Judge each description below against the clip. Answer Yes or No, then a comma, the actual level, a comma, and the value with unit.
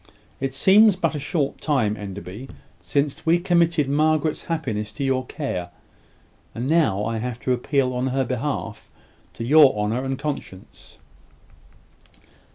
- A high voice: No, low, 135 Hz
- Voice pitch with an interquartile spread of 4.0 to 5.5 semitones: Yes, average, 5.1 semitones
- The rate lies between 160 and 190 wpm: No, average, 140 wpm